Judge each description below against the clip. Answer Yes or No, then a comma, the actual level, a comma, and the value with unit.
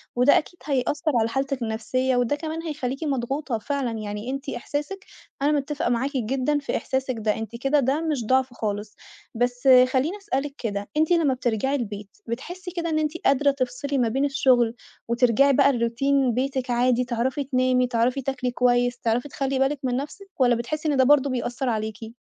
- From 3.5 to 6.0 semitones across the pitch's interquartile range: No, average, 2.8 semitones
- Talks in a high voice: Yes, very high, 260 Hz